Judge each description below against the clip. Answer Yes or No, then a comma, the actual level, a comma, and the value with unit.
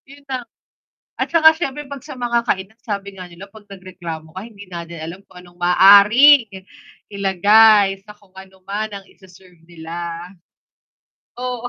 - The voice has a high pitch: Yes, high, 200 Hz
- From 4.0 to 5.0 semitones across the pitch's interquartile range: Yes, average, 4.3 semitones